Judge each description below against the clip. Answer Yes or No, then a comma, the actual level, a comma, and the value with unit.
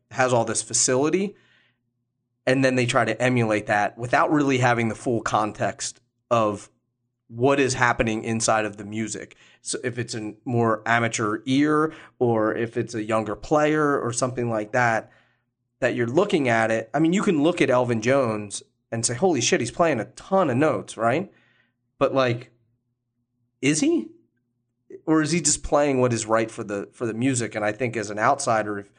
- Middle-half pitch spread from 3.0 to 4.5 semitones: No, narrow, 2.5 semitones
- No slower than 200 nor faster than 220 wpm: No, average, 185 wpm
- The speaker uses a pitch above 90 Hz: Yes, low, 120 Hz